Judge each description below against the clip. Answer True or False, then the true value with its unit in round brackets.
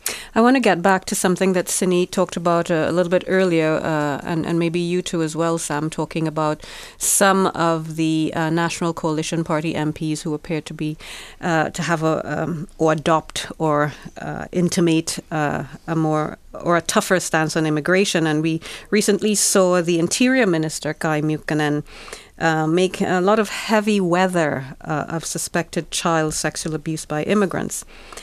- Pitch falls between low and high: True (165 Hz)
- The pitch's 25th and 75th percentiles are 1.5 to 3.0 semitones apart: True (2.6 semitones)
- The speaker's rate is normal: False (175 wpm)